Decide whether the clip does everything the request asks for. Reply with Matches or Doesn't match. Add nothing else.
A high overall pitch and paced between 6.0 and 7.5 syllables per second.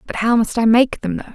Matches